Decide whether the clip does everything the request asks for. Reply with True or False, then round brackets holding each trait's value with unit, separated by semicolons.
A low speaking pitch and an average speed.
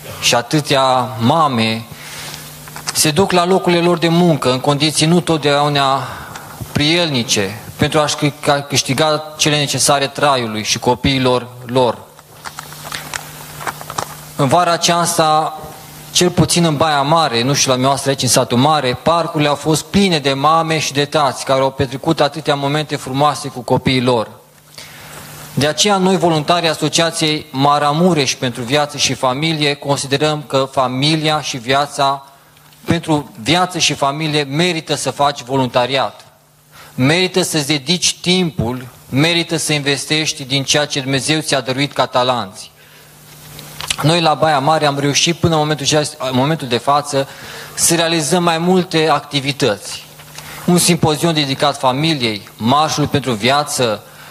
False (145 Hz; 130 wpm)